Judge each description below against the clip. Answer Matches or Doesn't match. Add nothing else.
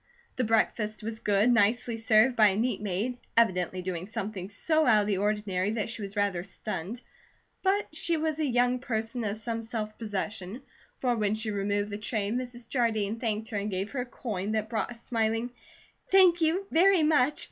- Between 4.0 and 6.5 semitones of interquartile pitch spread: Doesn't match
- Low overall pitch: Doesn't match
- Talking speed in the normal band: Matches